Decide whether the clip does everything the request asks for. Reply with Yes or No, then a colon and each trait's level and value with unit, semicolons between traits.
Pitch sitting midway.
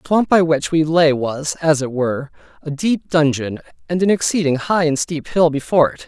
Yes: medium, 155 Hz